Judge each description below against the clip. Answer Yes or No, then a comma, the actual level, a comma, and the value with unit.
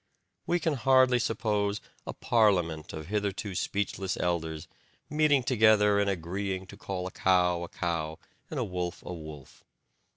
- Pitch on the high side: No, very low, 95 Hz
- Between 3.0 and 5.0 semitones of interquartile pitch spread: Yes, average, 3.8 semitones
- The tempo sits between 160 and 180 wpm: No, average, 150 wpm